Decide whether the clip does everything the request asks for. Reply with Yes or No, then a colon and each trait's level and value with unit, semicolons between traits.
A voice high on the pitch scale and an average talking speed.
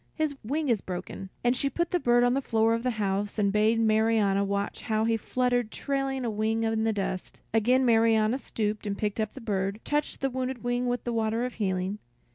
No: high, 225 Hz; fast, 220 wpm